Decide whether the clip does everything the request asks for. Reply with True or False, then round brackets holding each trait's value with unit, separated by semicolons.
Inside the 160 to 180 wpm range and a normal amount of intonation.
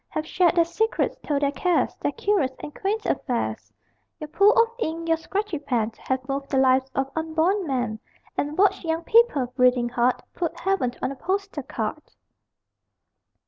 False (170 wpm; 6.1 semitones)